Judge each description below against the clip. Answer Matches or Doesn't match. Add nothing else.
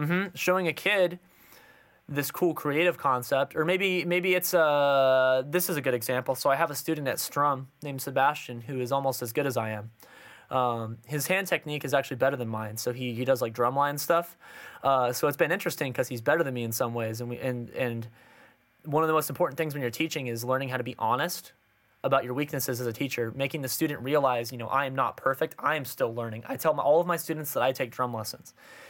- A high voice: Doesn't match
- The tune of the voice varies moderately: Matches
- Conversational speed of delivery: Doesn't match